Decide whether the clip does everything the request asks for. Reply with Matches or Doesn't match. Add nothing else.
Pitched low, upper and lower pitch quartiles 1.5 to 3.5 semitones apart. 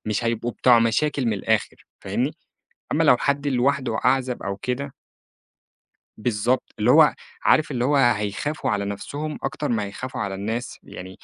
Doesn't match